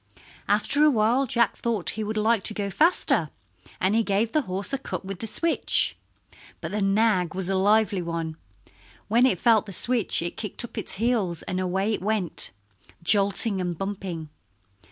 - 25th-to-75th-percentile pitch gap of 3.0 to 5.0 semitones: Yes, average, 3.4 semitones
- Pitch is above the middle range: Yes, high, 205 Hz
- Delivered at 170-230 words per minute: Yes, average, 175 wpm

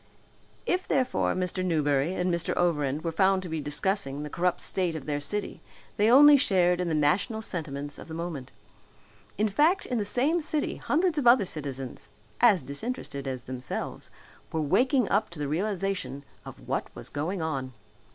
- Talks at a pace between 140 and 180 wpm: Yes, average, 175 wpm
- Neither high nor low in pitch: Yes, medium, 175 Hz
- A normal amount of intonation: No, wide, 6.4 semitones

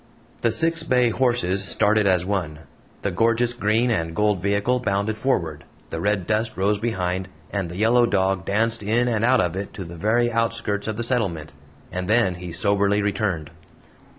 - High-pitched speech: No, low, 105 Hz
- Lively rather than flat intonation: No, average, 3.5 semitones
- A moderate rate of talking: Yes, average, 180 wpm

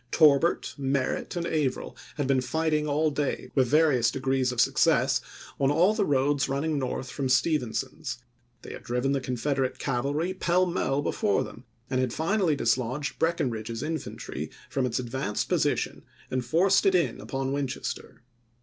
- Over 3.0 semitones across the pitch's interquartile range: Yes, average, 3.6 semitones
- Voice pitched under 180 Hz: Yes, medium, 140 Hz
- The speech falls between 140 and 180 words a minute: Yes, average, 160 wpm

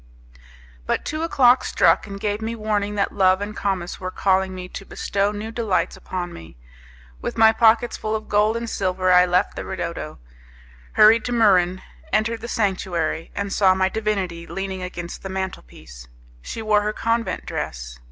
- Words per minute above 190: No, average, 170 wpm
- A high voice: Yes, high, 200 Hz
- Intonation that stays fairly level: No, average, 3.0 semitones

